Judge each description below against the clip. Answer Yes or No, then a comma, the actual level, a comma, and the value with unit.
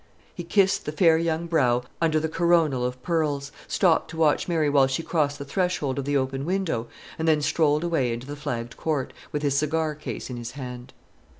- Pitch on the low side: No, medium, 150 Hz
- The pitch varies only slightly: No, average, 3.5 semitones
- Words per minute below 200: No, fast, 205 wpm